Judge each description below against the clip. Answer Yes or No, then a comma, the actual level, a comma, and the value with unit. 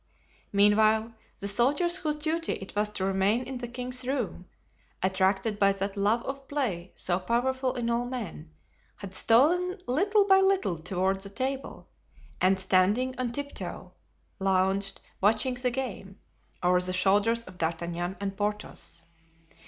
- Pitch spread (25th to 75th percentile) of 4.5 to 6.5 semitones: Yes, average, 5.1 semitones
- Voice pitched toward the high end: Yes, high, 215 Hz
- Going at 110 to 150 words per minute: Yes, average, 145 wpm